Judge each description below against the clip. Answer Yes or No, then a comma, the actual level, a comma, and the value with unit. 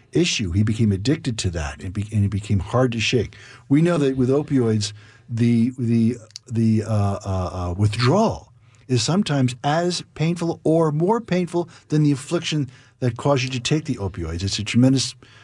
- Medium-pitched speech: No, low, 120 Hz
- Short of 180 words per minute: Yes, average, 170 wpm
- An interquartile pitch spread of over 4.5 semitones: Yes, average, 5.2 semitones